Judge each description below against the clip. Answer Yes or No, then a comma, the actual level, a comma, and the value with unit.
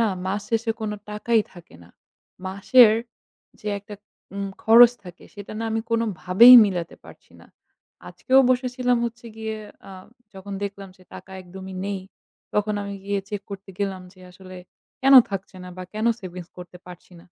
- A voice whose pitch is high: Yes, high, 200 Hz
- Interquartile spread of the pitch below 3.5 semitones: Yes, average, 3.1 semitones